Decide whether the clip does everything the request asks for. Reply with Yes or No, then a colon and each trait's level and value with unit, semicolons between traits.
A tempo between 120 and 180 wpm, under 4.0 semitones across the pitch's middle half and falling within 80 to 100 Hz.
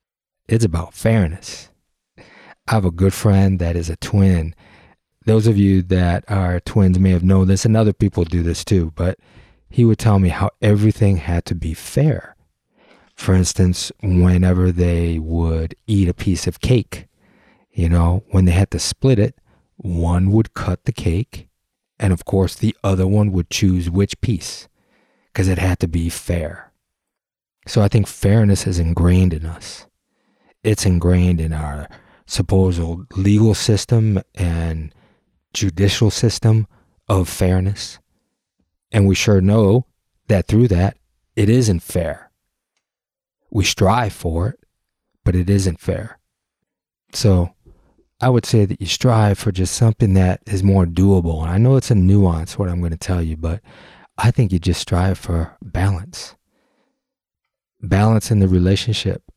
Yes: average, 155 wpm; average, 3.1 semitones; very low, 95 Hz